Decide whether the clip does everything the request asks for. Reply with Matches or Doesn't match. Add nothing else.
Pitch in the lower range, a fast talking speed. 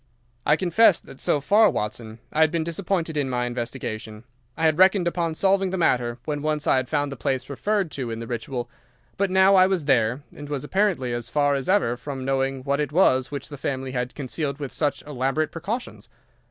Doesn't match